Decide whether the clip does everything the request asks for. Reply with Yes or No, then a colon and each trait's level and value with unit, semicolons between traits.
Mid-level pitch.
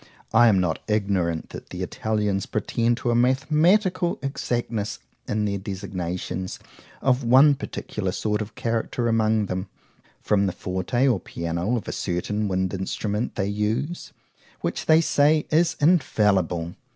No: low, 105 Hz